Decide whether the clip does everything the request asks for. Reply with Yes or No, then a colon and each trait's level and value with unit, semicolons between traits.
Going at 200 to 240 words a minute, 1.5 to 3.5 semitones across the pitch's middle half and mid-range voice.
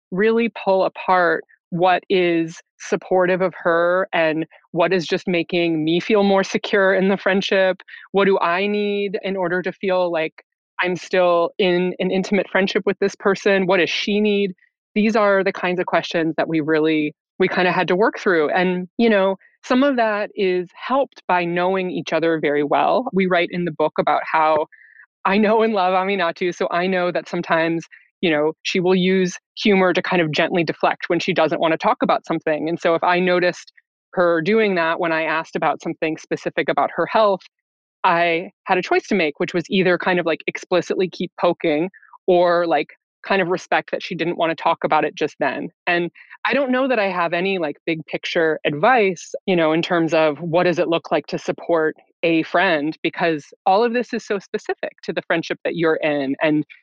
Yes: fast, 205 wpm; narrow, 2.5 semitones; medium, 180 Hz